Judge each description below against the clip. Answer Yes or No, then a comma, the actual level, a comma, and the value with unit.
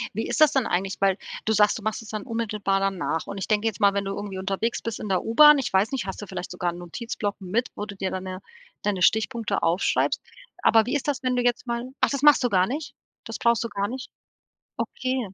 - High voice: Yes, high, 215 Hz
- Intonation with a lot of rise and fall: No, average, 3.6 semitones